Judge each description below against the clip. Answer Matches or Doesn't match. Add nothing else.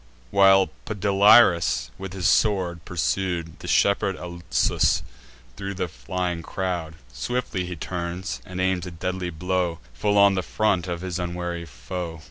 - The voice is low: Matches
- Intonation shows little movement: Matches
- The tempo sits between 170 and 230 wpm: Doesn't match